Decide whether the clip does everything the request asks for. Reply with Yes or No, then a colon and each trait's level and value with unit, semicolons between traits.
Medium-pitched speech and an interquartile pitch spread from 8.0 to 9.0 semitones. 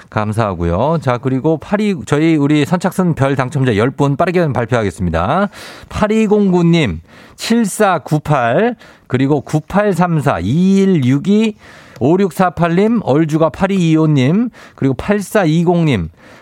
No: medium, 160 Hz; wide, 6.4 semitones